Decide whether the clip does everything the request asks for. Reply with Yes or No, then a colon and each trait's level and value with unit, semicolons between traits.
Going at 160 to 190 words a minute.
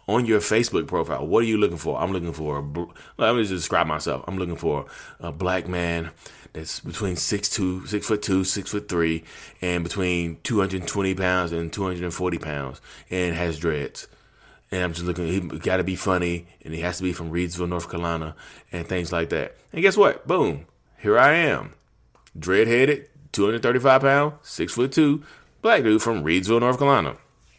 No: average, 200 wpm